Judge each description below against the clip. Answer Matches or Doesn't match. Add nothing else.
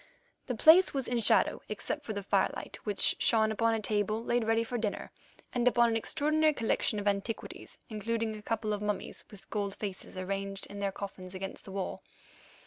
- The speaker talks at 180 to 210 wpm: Matches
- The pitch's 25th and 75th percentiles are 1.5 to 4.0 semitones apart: Matches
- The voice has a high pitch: Matches